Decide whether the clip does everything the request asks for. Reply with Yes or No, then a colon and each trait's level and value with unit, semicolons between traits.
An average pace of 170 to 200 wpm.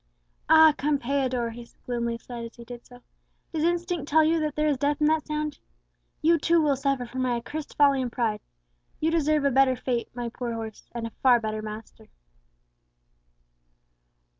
Yes: average, 180 wpm